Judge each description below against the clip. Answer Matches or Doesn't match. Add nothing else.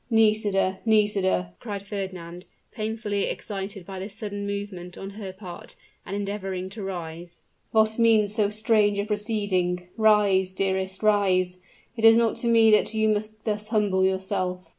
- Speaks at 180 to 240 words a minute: Doesn't match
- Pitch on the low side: Doesn't match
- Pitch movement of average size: Doesn't match